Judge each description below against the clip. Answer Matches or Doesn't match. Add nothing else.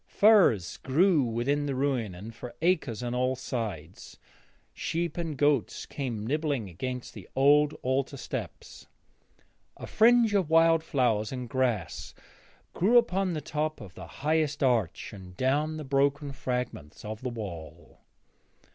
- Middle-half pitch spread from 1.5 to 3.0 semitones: Doesn't match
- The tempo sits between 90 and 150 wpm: Matches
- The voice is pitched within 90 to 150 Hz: Matches